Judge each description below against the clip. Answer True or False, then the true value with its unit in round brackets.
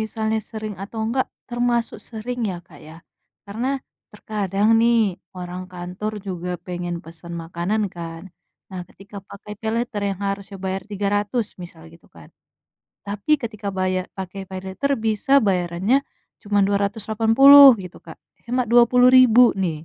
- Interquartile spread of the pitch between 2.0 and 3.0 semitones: False (3.7 semitones)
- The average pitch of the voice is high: True (205 Hz)